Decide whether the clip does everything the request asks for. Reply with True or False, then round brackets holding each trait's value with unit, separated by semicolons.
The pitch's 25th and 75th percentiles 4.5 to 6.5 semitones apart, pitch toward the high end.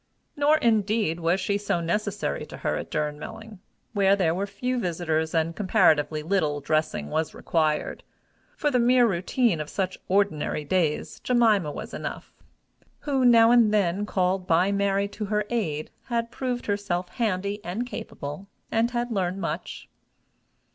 True (5.2 semitones; 200 Hz)